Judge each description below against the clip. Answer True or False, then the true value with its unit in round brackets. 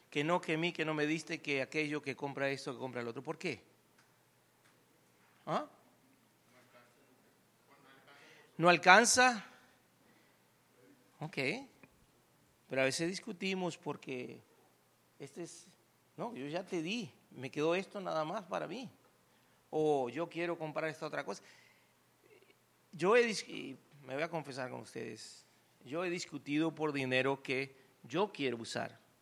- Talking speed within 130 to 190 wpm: True (135 wpm)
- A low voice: False (155 Hz)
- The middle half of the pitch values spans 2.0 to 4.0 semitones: False (4.4 semitones)